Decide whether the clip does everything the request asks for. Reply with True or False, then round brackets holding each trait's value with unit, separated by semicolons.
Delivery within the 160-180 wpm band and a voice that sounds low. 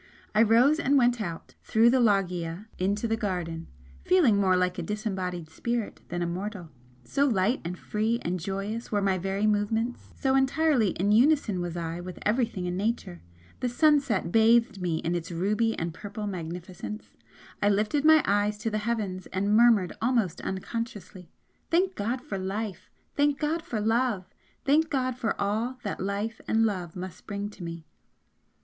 False (170 wpm; 210 Hz)